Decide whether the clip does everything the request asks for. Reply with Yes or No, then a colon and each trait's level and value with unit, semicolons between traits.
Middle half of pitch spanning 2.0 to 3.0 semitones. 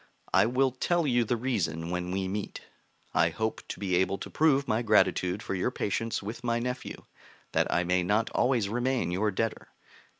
No: average, 4.7 semitones